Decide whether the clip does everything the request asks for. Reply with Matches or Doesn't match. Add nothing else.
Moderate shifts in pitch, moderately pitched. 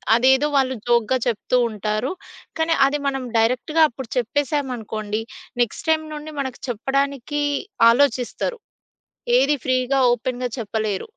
Doesn't match